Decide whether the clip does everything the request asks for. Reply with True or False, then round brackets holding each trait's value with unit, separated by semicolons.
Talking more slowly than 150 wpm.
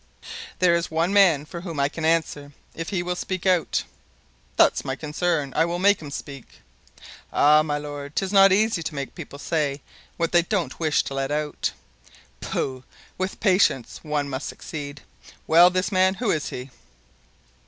False (175 wpm)